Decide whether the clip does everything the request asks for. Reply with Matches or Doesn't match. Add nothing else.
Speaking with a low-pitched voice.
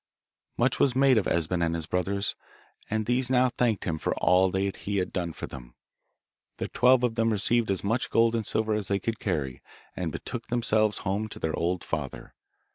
Matches